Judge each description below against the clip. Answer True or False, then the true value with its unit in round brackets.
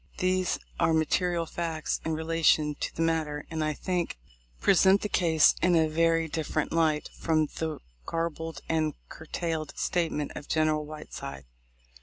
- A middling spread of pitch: False (1.3 semitones)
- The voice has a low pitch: False (160 Hz)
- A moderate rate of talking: True (155 wpm)